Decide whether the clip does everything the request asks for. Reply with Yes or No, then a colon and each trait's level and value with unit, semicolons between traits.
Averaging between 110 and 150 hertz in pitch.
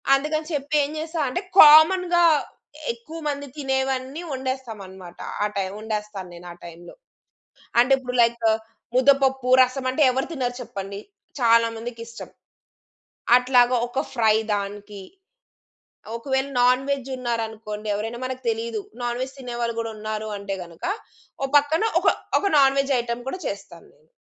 No: high, 245 Hz